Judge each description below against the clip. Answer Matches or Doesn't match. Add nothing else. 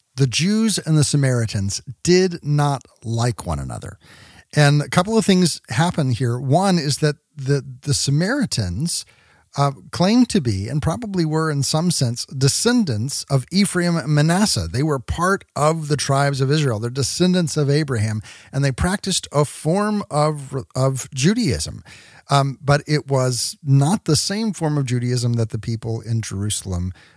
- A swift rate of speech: Doesn't match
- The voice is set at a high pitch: Doesn't match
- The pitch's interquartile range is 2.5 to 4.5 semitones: Doesn't match